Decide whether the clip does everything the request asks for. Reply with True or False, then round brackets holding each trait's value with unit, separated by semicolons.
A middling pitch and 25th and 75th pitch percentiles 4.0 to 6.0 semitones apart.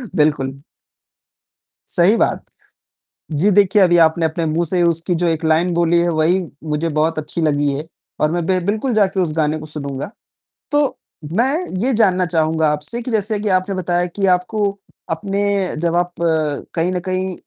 False (170 Hz; 3.3 semitones)